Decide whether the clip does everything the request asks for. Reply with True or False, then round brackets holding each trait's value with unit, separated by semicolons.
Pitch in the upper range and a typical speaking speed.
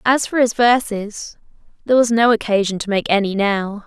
True (220 Hz; 185 wpm)